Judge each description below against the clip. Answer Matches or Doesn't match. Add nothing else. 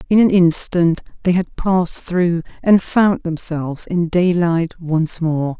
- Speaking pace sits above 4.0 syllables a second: Doesn't match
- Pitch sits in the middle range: Matches